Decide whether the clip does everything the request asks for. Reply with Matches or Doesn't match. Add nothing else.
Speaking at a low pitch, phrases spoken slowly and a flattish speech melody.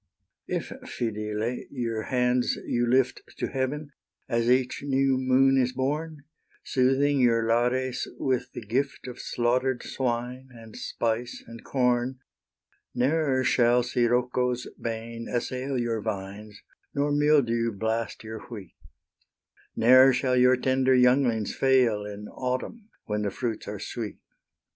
Matches